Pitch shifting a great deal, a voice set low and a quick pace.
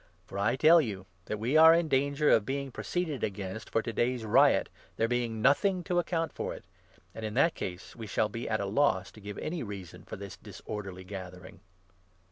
Yes: wide, 6.1 semitones; low, 115 Hz; fast, 215 wpm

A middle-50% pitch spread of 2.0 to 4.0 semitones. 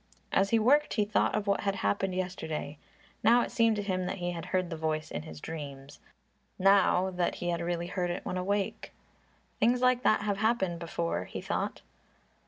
Yes: average, 3.5 semitones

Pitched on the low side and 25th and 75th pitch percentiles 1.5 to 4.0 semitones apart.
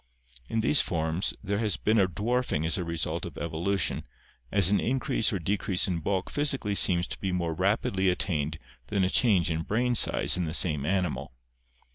Yes: very low, 95 Hz; average, 3.7 semitones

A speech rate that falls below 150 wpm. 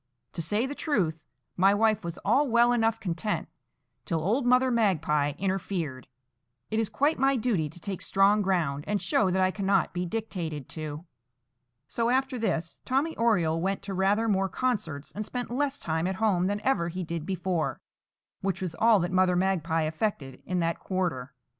No: average, 180 wpm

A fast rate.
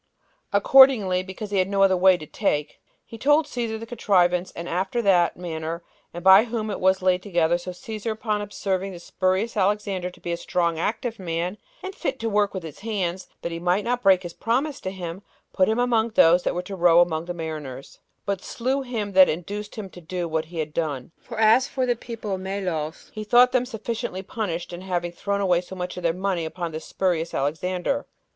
Yes: fast, 215 wpm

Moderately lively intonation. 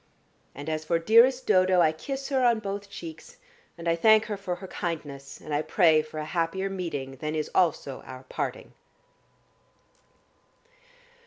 Yes: average, 4.3 semitones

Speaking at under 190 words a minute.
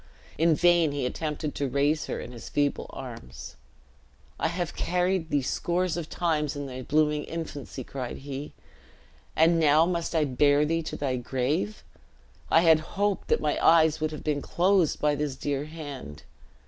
Yes: average, 170 wpm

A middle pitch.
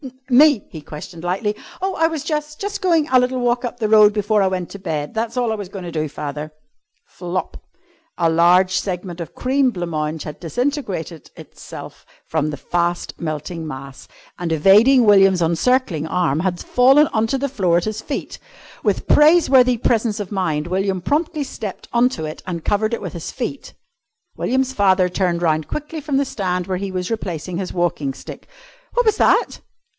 No: high, 195 Hz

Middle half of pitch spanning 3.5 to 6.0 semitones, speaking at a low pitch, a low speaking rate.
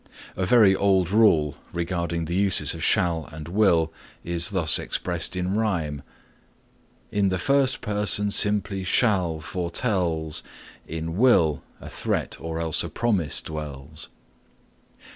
Yes: average, 4.0 semitones; very low, 90 Hz; slow, 125 wpm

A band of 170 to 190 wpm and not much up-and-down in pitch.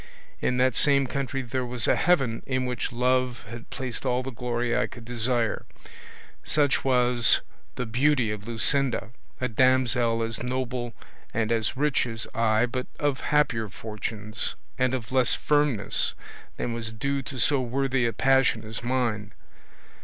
No: average, 155 wpm; narrow, 2.3 semitones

